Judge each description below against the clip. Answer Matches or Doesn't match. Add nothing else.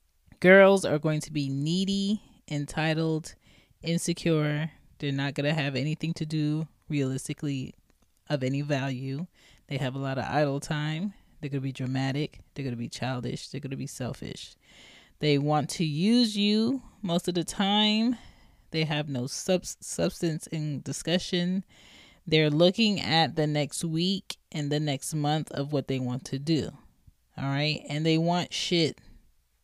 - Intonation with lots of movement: Doesn't match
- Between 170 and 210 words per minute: Doesn't match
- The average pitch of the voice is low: Doesn't match